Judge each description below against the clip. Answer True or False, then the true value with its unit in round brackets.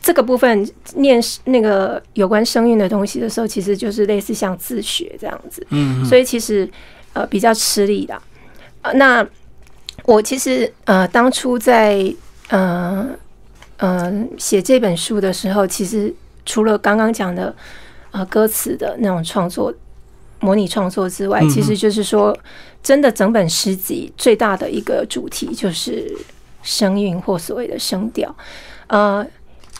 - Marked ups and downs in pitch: False (3.9 semitones)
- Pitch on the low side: False (210 Hz)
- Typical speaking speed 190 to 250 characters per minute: True (220 characters per minute)